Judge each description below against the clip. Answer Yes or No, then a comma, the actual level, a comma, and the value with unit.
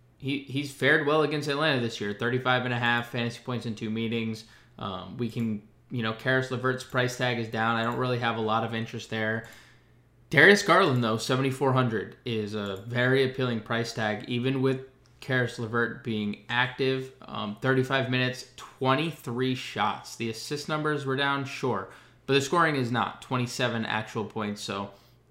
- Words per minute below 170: No, average, 175 wpm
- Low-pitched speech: Yes, low, 125 Hz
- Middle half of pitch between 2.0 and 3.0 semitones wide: Yes, narrow, 2.4 semitones